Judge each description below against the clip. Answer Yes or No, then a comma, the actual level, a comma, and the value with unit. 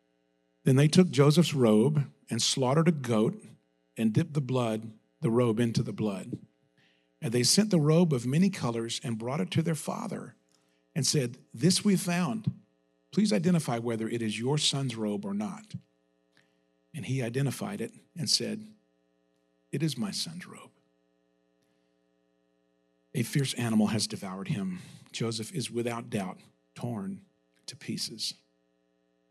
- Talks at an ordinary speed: Yes, average, 145 wpm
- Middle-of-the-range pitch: No, low, 115 Hz